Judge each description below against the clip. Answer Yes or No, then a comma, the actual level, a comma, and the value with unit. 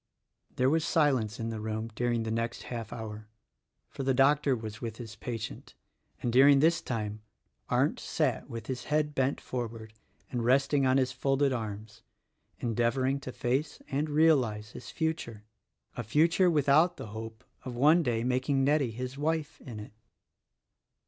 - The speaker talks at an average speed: Yes, average, 160 wpm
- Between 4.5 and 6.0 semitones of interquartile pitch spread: No, average, 4.0 semitones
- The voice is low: Yes, low, 125 Hz